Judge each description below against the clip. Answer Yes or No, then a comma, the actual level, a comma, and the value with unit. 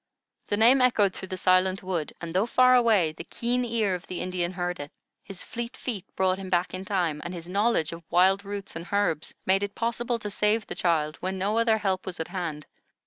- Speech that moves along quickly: Yes, fast, 225 wpm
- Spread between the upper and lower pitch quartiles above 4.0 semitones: No, average, 3.6 semitones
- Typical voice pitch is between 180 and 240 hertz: Yes, high, 190 Hz